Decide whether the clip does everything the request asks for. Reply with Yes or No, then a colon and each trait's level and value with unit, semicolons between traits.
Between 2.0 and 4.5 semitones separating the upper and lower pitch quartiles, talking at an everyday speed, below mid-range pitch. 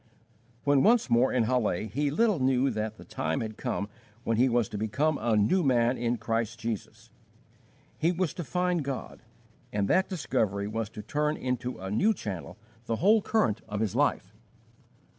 No: wide, 5.6 semitones; average, 180 wpm; low, 120 Hz